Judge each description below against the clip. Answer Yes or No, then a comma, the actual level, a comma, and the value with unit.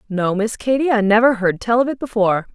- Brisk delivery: Yes, fast, 235 wpm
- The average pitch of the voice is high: Yes, high, 220 Hz